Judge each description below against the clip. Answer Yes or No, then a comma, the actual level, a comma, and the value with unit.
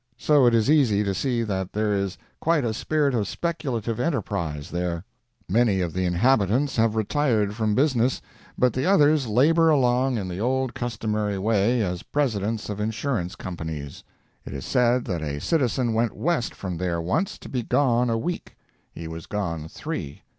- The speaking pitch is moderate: No, low, 110 Hz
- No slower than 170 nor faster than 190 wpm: Yes, average, 175 wpm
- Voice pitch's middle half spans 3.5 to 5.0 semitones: No, wide, 5.5 semitones